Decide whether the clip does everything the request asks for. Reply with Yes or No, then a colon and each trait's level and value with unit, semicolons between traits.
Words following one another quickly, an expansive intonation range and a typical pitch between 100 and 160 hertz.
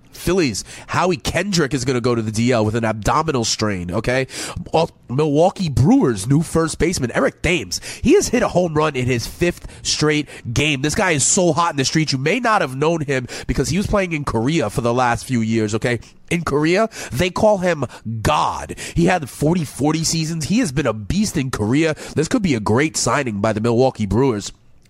Yes: fast, 210 wpm; wide, 5.7 semitones; medium, 140 Hz